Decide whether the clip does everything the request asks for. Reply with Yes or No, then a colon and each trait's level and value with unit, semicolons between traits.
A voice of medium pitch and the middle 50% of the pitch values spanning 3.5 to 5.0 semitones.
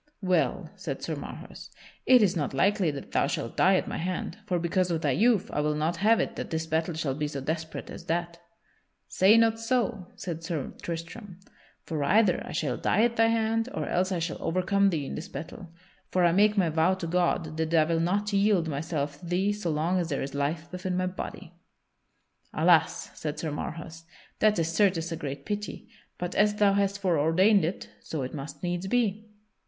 Yes: medium, 175 Hz; average, 3.8 semitones